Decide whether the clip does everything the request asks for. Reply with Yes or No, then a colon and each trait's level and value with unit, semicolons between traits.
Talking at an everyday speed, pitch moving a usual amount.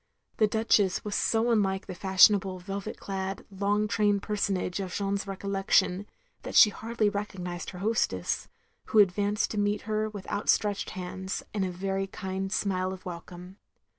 No: average, 160 wpm; narrow, 1.7 semitones